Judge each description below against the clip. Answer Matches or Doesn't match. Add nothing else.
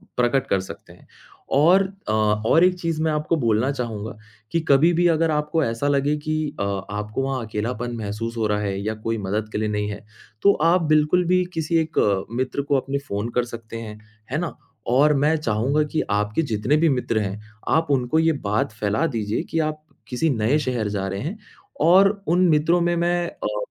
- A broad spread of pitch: Matches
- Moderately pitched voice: Doesn't match